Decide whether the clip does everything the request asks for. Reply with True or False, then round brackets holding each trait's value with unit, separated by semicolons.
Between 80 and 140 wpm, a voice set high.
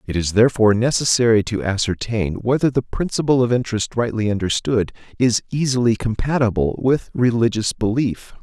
False (135 wpm; 115 Hz)